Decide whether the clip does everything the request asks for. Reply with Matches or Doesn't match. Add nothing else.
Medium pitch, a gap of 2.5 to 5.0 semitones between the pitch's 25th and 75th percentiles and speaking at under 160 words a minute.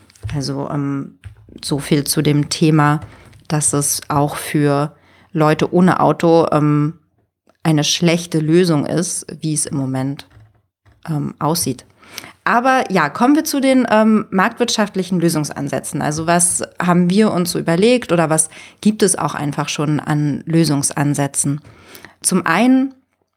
Matches